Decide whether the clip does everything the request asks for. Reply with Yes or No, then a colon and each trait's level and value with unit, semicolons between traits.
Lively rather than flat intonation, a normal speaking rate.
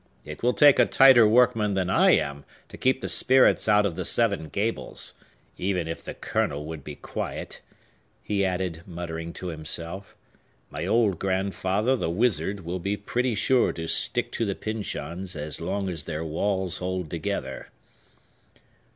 No: average, 4.4 semitones; average, 160 wpm